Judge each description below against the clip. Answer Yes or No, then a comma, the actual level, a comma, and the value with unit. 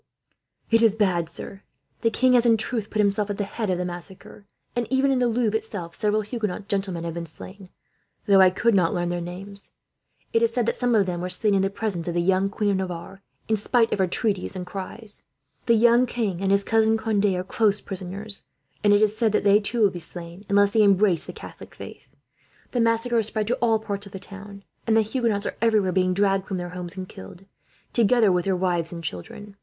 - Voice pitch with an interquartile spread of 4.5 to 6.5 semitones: No, average, 3.2 semitones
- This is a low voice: No, high, 200 Hz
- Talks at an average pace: No, fast, 235 wpm